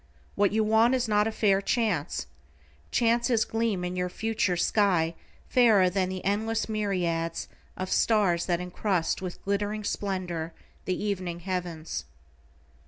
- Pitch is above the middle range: Yes, high, 195 Hz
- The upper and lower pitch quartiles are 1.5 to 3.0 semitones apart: No, average, 3.4 semitones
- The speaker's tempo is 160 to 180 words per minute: No, slow, 135 wpm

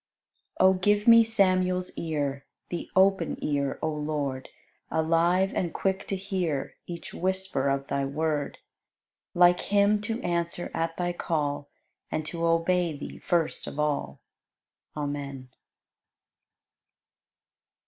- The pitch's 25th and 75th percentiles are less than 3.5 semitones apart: No, average, 4.3 semitones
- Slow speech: Yes, slow, 120 wpm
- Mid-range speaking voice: Yes, medium, 170 Hz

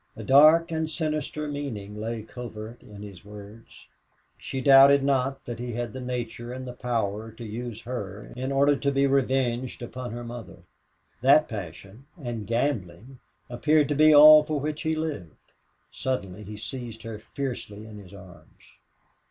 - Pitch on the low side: Yes, low, 125 Hz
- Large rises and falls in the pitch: No, average, 4.4 semitones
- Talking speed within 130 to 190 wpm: Yes, average, 160 wpm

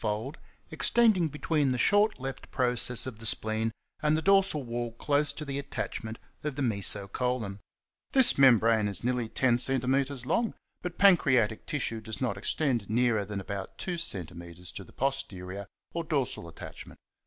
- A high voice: No, low, 125 Hz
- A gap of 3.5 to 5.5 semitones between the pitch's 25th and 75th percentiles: Yes, average, 5.0 semitones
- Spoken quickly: No, average, 165 wpm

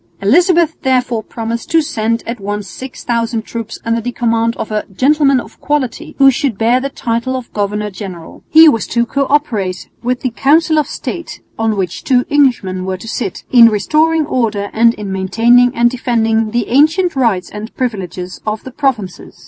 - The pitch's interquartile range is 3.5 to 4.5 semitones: Yes, average, 3.9 semitones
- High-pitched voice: Yes, high, 235 Hz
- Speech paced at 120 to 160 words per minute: No, average, 180 wpm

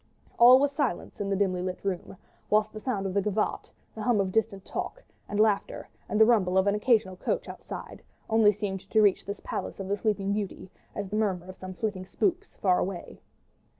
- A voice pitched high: Yes, high, 205 Hz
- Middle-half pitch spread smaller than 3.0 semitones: Yes, narrow, 2.5 semitones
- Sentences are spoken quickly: Yes, fast, 210 wpm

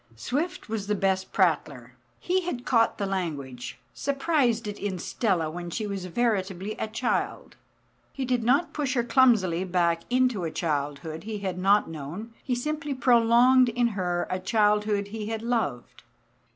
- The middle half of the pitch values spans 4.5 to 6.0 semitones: Yes, average, 5.3 semitones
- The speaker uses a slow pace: No, average, 160 wpm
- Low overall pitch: No, high, 210 Hz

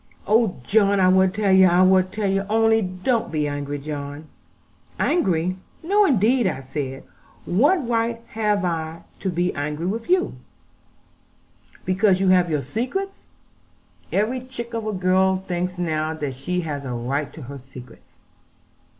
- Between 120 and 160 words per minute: Yes, average, 155 wpm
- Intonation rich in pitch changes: Yes, wide, 5.9 semitones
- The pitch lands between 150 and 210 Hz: Yes, medium, 185 Hz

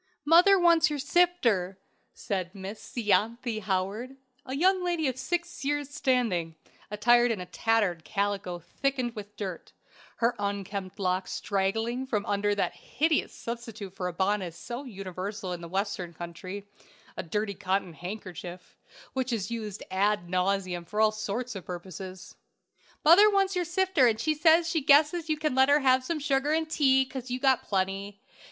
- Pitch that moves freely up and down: Yes, wide, 6.3 semitones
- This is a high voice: Yes, high, 220 Hz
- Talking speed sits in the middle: Yes, average, 160 wpm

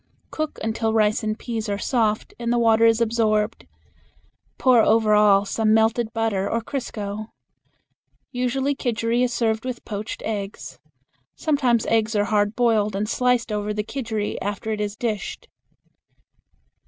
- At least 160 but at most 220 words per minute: No, average, 145 wpm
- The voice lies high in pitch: Yes, high, 220 Hz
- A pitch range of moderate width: No, narrow, 2.0 semitones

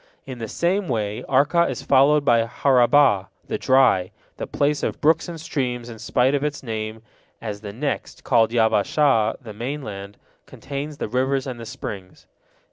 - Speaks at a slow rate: No, average, 165 wpm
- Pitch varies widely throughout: No, average, 4.4 semitones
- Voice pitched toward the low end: Yes, low, 125 Hz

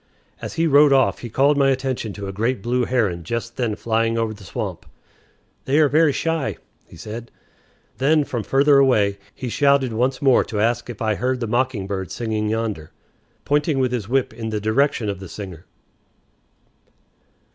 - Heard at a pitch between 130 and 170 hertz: No, low, 120 Hz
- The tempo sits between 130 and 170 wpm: No, average, 180 wpm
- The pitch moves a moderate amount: Yes, average, 4.0 semitones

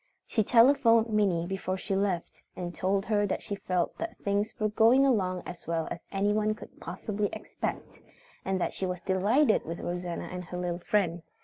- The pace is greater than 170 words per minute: Yes, average, 185 wpm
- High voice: Yes, high, 195 Hz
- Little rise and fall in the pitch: No, average, 3.1 semitones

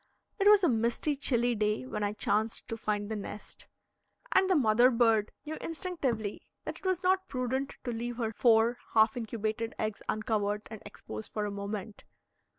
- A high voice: Yes, high, 225 Hz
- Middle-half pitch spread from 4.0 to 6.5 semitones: No, average, 3.4 semitones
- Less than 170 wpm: No, average, 175 wpm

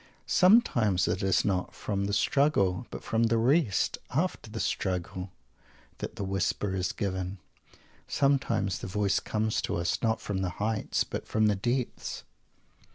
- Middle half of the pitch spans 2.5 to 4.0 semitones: Yes, average, 3.5 semitones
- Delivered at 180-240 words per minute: No, average, 155 wpm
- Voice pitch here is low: Yes, low, 105 Hz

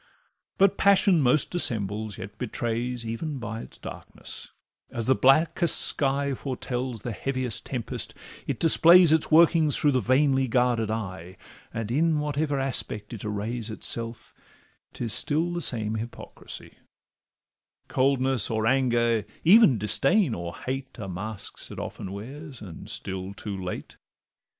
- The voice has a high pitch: No, low, 125 Hz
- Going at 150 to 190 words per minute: No, slow, 135 wpm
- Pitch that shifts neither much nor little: Yes, average, 4.8 semitones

